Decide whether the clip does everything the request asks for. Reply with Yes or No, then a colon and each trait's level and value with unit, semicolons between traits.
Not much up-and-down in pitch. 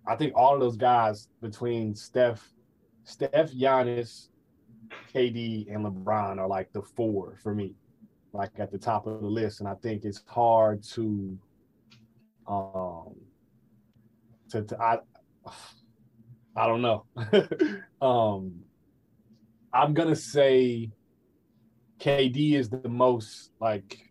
Yes: narrow, 2.3 semitones